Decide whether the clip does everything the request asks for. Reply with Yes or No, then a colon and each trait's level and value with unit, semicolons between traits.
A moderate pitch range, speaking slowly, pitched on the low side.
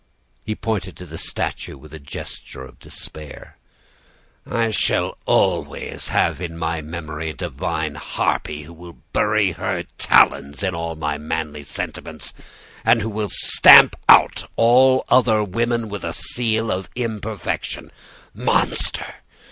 No: wide, 5.9 semitones; slow, 130 wpm; very low, 90 Hz